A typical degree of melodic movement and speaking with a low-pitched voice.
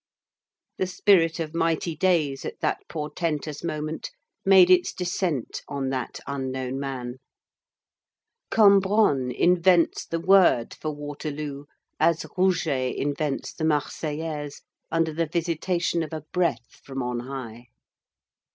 No: average, 3.7 semitones; medium, 155 Hz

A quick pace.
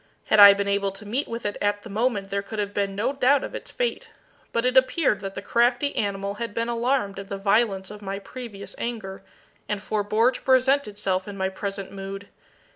Yes: fast, 215 wpm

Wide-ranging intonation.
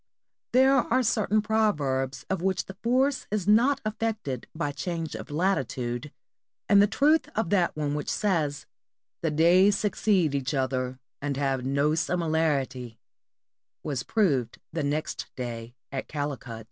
Yes: wide, 7.2 semitones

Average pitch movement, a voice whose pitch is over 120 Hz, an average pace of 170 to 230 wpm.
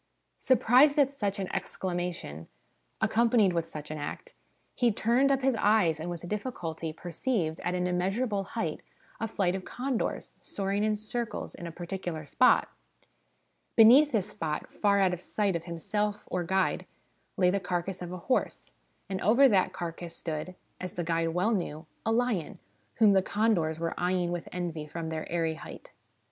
Yes: average, 4.4 semitones; medium, 185 Hz; average, 175 wpm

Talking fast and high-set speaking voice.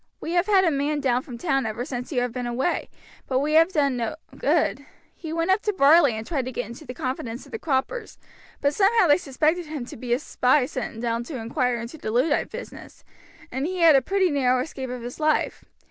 Yes: fast, 235 wpm; very high, 275 Hz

